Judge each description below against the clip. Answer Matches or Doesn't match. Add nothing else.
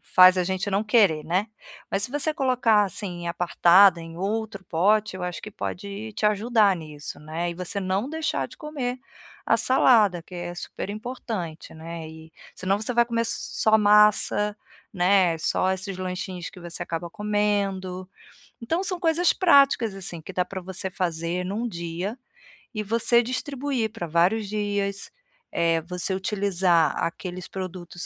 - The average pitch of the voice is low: Doesn't match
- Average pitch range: Matches